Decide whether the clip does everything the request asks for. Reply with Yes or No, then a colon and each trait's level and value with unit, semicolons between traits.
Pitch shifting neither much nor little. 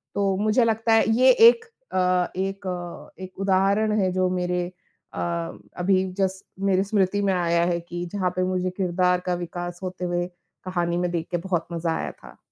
No: narrow, 1.9 semitones